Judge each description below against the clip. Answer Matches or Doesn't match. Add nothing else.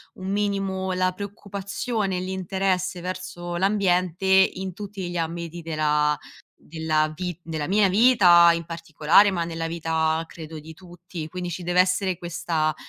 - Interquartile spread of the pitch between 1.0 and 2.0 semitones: Doesn't match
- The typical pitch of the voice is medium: Matches